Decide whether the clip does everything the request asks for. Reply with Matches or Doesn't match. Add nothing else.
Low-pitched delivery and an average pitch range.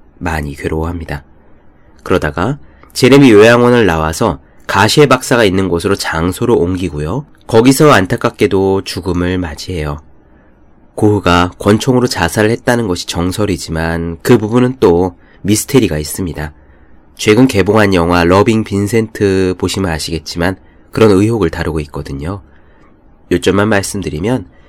Matches